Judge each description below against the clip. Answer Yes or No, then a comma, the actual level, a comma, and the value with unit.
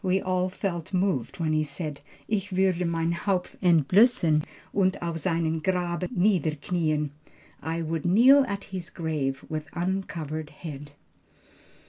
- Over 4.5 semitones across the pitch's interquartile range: No, average, 3.2 semitones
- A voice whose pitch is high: No, medium, 170 Hz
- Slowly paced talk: Yes, slow, 130 wpm